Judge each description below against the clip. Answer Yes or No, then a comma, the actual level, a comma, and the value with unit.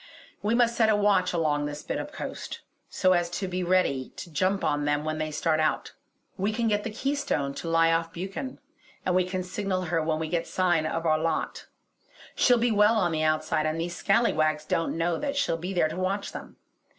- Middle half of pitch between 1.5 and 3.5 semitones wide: No, average, 4.3 semitones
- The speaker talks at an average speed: No, fast, 220 wpm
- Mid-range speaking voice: Yes, medium, 175 Hz